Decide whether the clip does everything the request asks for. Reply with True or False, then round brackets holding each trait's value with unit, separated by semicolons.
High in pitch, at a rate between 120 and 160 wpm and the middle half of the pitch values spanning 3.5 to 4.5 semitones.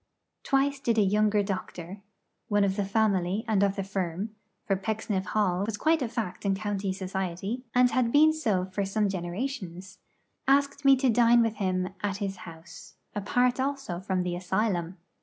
False (200 Hz; 175 wpm; 3.8 semitones)